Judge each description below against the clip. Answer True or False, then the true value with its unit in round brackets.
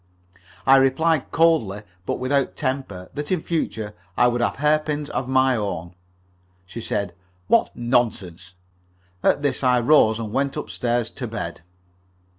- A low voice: True (125 Hz)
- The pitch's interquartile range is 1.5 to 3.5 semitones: False (4.9 semitones)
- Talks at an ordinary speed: True (145 wpm)